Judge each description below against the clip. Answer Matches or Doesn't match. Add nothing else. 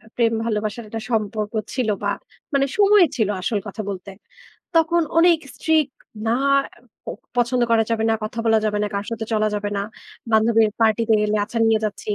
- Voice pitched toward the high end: Matches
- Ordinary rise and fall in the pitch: Doesn't match